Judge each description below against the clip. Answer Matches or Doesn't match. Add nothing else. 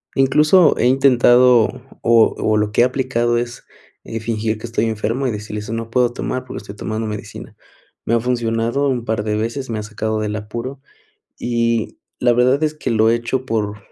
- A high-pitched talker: Doesn't match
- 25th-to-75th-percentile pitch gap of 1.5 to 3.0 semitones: Matches